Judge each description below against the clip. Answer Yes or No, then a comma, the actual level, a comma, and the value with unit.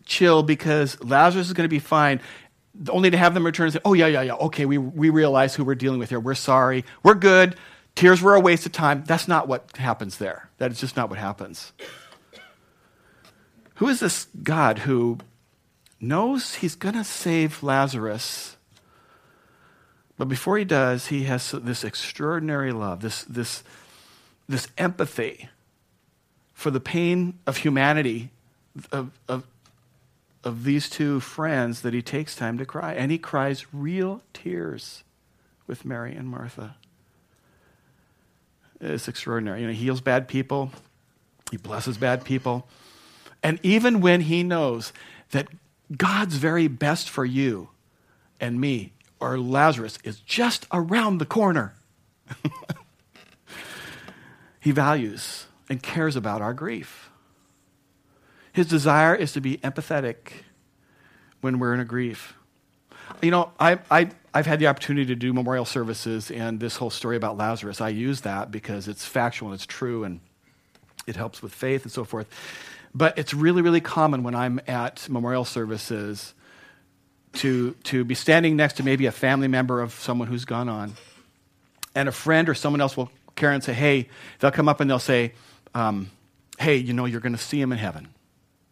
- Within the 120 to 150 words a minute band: No, average, 160 wpm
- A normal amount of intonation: Yes, average, 4.6 semitones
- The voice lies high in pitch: No, low, 135 Hz